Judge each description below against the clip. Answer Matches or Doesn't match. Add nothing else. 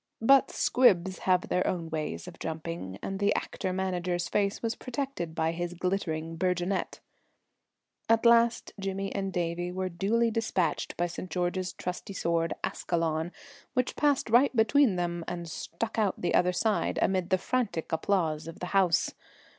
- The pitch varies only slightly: Doesn't match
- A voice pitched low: Doesn't match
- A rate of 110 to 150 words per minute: Doesn't match